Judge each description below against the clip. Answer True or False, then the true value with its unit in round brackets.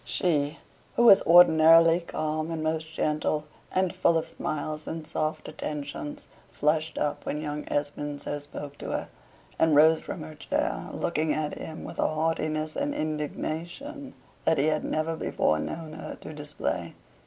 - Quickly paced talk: False (160 wpm)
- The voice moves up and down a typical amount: False (1.4 semitones)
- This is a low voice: False (155 Hz)